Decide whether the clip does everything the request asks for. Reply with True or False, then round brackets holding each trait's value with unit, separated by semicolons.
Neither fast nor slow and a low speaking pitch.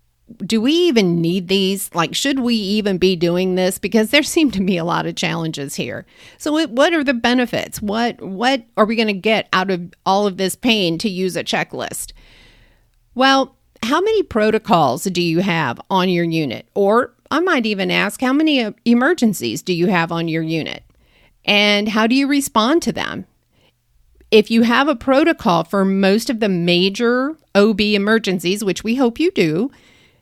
False (185 wpm; 205 Hz)